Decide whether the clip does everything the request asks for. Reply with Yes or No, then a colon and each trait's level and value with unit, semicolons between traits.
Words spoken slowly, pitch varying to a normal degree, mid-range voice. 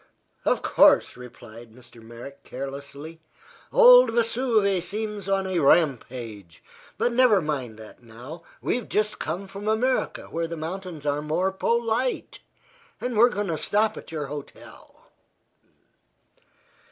No: slow, 130 wpm; wide, 7.6 semitones; medium, 170 Hz